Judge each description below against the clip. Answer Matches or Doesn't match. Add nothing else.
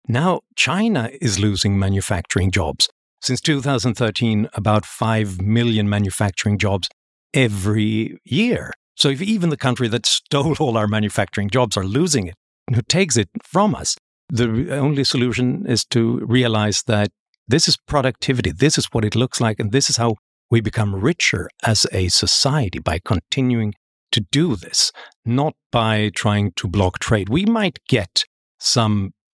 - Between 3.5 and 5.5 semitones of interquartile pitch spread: Matches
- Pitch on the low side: Matches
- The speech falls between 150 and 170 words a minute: Matches